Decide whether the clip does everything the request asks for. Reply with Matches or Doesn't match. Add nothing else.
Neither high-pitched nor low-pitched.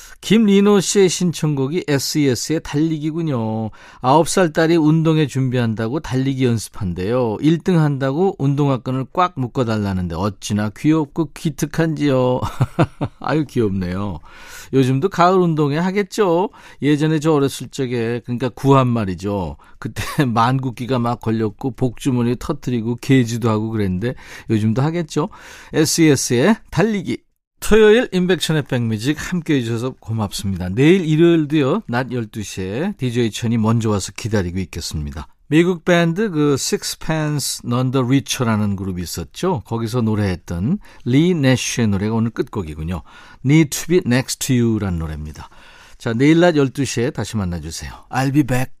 Doesn't match